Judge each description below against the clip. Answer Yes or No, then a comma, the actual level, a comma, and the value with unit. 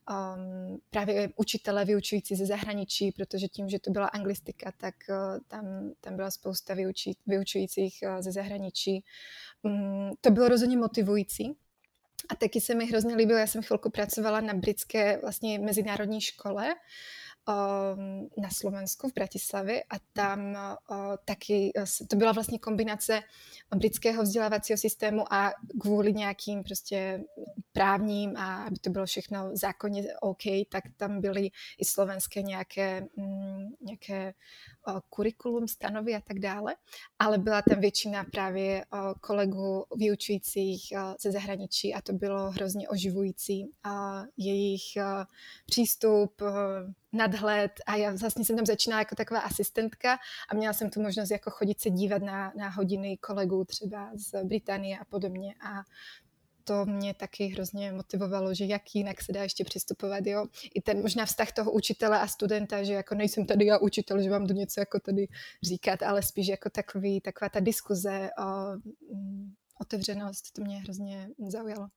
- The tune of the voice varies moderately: No, narrow, 1.4 semitones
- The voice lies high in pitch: Yes, high, 200 Hz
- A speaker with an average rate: Yes, average, 145 wpm